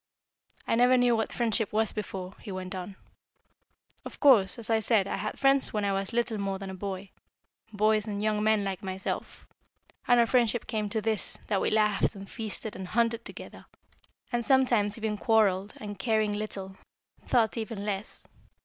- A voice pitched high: Yes, high, 215 Hz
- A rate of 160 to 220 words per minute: Yes, average, 180 wpm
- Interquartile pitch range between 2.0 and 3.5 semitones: Yes, narrow, 2.4 semitones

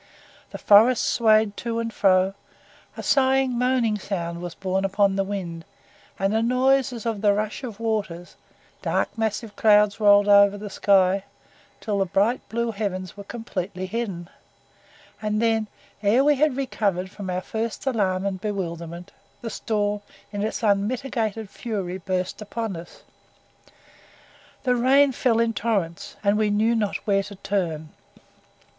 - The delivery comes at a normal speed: Yes, average, 150 wpm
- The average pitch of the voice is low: No, high, 210 Hz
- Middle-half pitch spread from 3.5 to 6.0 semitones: No, average, 3.0 semitones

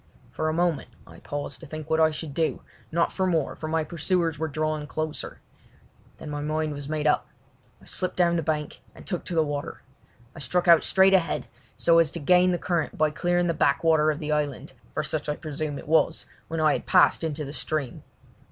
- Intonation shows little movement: Yes, narrow, 1.9 semitones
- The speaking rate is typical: No, fast, 215 wpm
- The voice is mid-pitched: Yes, medium, 155 Hz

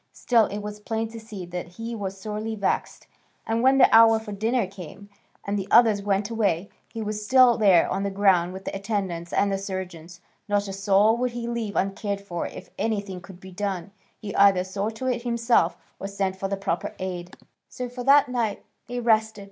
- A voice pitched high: Yes, high, 205 Hz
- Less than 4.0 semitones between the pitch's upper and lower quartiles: Yes, average, 2.7 semitones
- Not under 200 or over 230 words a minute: Yes, fast, 205 wpm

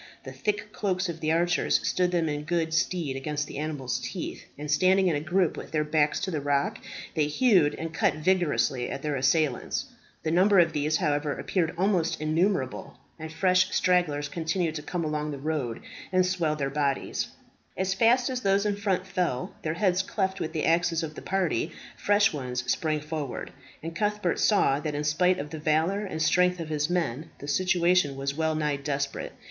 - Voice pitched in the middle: Yes, medium, 160 Hz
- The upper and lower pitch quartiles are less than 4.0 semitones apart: Yes, average, 3.6 semitones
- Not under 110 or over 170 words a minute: No, average, 195 wpm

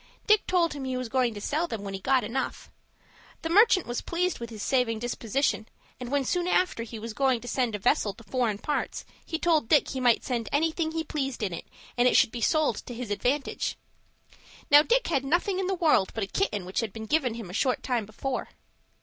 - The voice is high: Yes, very high, 255 Hz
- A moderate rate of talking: No, fast, 230 wpm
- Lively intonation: Yes, wide, 5.7 semitones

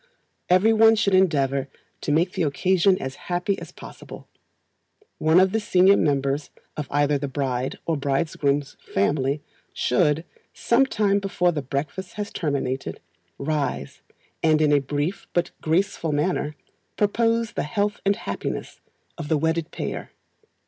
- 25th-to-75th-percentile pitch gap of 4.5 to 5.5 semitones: Yes, average, 5.2 semitones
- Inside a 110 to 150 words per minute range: Yes, slow, 135 wpm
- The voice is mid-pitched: Yes, medium, 155 Hz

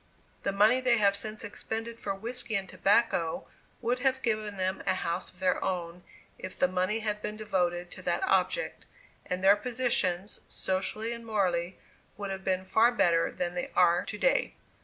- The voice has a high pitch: Yes, high, 200 Hz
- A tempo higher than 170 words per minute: Yes, average, 180 wpm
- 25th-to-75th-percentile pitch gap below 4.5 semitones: Yes, average, 3.7 semitones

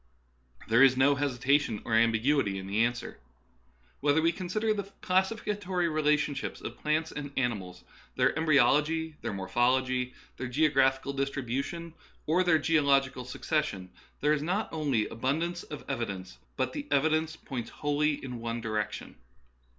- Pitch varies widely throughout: No, average, 4.5 semitones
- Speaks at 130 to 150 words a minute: Yes, average, 145 wpm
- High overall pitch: No, medium, 140 Hz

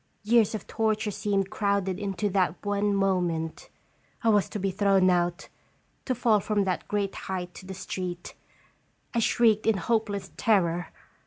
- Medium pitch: No, high, 200 Hz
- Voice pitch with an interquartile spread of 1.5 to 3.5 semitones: Yes, narrow, 2.5 semitones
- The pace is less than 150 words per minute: No, average, 155 wpm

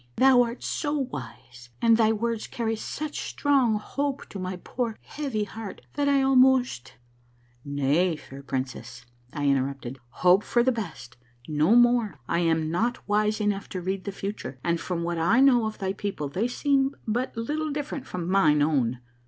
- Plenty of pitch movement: Yes, wide, 8.5 semitones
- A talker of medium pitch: No, high, 205 Hz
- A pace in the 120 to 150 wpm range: No, average, 175 wpm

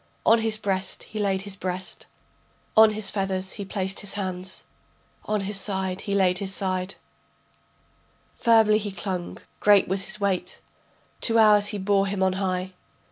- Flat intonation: Yes, narrow, 1.7 semitones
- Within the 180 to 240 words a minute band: No, average, 155 wpm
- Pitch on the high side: Yes, high, 195 Hz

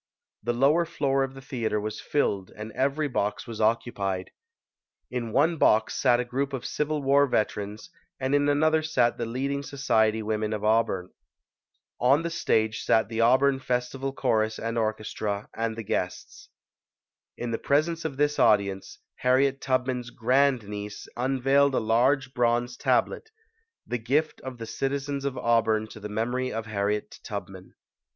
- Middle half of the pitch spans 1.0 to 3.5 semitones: No, average, 4.0 semitones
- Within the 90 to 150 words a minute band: No, average, 160 wpm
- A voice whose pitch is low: Yes, low, 125 Hz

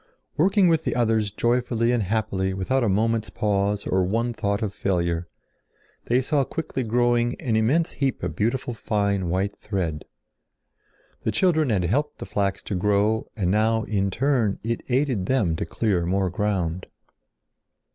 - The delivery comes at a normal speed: Yes, average, 155 wpm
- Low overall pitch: Yes, low, 110 Hz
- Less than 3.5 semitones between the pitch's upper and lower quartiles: No, average, 3.9 semitones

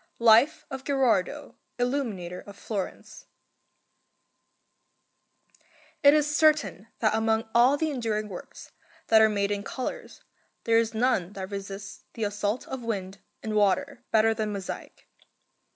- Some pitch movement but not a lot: Yes, average, 4.1 semitones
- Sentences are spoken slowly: Yes, slow, 125 wpm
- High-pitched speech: Yes, high, 220 Hz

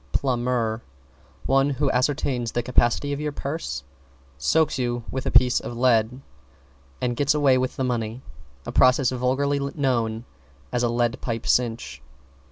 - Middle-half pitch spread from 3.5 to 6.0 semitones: No, narrow, 2.5 semitones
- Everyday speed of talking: Yes, average, 150 wpm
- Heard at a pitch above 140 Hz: No, low, 125 Hz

